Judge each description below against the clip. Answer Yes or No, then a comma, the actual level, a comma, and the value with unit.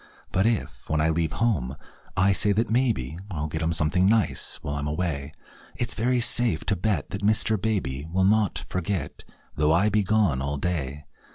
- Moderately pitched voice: No, very low, 90 Hz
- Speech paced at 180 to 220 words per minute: Yes, average, 185 wpm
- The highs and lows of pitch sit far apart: Yes, wide, 5.9 semitones